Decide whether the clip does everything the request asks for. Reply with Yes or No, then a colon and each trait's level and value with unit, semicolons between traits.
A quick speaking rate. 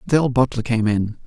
Yes: fast, 235 wpm